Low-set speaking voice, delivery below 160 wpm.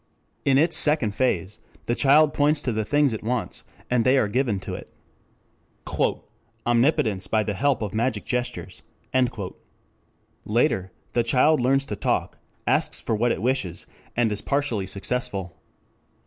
Yes: low, 120 Hz; average, 150 wpm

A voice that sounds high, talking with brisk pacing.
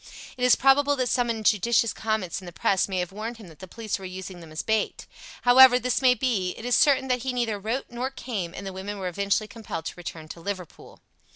Yes: high, 215 Hz; fast, 245 wpm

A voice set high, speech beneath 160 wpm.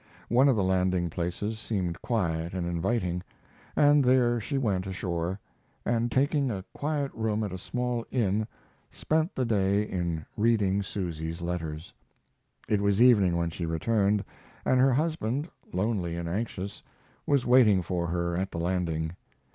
No: low, 100 Hz; average, 150 wpm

